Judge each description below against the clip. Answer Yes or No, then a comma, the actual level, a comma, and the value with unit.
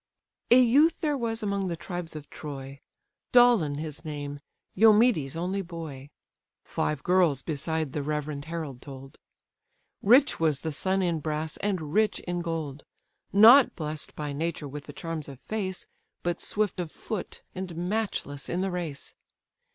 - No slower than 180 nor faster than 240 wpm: No, average, 150 wpm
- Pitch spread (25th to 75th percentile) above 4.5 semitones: Yes, average, 4.9 semitones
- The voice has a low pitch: No, medium, 165 Hz